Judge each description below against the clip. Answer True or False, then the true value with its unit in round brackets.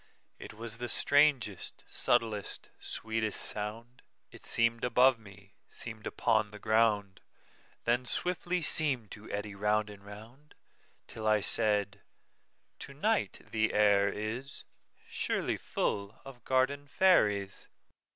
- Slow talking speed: True (105 wpm)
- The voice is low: True (110 Hz)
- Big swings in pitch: False (3.0 semitones)